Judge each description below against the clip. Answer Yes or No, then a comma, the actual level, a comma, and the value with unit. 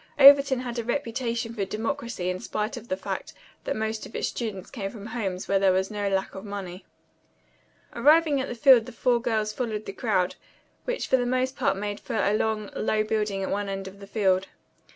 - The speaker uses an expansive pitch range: No, average, 3.7 semitones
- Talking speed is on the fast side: Yes, fast, 215 wpm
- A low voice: No, high, 215 Hz